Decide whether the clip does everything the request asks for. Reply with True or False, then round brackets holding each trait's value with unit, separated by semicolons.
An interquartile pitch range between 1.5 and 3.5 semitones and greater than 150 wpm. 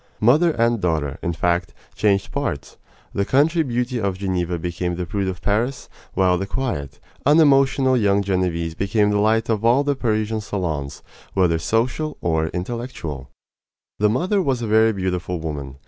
False (5.6 semitones; 160 wpm)